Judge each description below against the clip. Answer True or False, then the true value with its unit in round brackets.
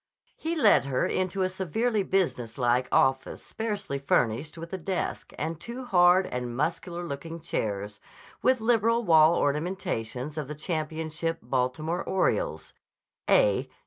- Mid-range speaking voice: True (165 Hz)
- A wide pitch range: True (5.7 semitones)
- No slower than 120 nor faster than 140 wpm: True (135 wpm)